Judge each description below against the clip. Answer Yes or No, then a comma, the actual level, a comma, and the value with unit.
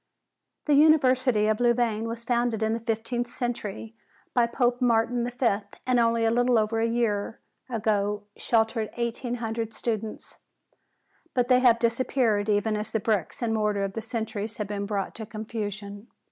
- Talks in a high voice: Yes, high, 225 Hz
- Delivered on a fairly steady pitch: Yes, narrow, 2.1 semitones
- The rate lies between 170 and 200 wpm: No, average, 160 wpm